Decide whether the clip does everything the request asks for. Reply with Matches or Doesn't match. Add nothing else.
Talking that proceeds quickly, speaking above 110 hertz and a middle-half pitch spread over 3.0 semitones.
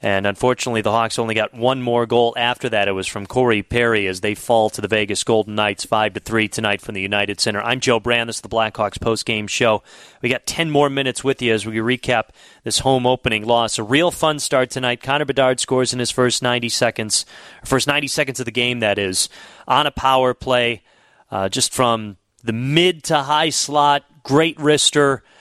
Matches